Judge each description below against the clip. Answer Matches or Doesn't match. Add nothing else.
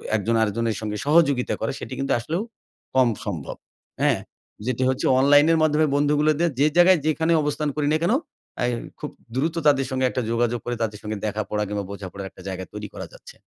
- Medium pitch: Doesn't match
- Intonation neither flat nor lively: Doesn't match